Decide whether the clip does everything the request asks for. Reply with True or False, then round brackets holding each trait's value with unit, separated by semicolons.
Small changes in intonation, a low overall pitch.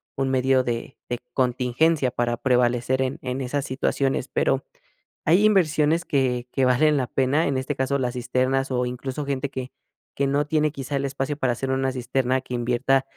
True (1.7 semitones; 130 Hz)